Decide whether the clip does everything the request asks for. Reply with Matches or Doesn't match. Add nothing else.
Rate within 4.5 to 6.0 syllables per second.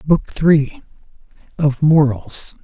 Doesn't match